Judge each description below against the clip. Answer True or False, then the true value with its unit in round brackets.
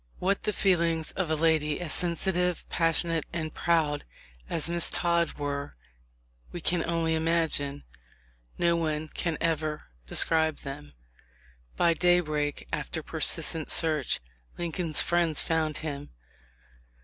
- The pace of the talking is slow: True (125 wpm)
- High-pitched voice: False (160 Hz)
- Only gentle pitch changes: True (2.0 semitones)